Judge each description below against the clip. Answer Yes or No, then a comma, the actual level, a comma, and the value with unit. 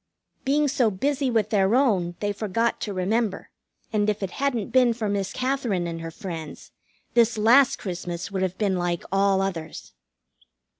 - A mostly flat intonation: No, average, 4.1 semitones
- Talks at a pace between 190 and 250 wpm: No, average, 165 wpm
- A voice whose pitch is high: Yes, high, 205 Hz